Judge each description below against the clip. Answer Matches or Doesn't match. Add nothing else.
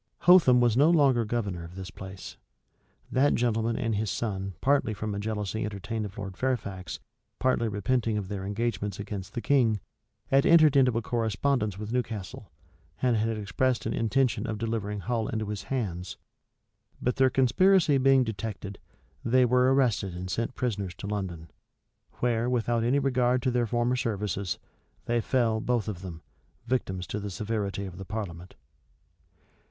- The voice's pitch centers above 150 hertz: Doesn't match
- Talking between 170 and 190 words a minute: Doesn't match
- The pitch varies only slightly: Doesn't match